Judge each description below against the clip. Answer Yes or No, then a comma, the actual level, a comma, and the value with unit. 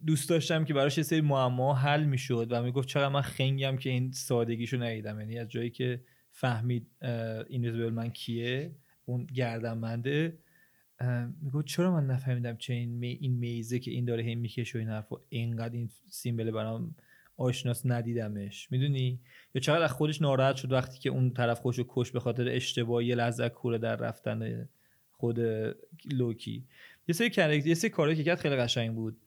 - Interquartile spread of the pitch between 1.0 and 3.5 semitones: Yes, average, 2.9 semitones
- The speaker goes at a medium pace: No, fast, 170 wpm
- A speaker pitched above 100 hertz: Yes, low, 125 Hz